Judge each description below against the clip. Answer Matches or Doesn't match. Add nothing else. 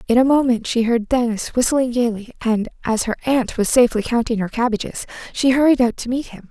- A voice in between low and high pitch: Doesn't match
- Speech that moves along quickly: Matches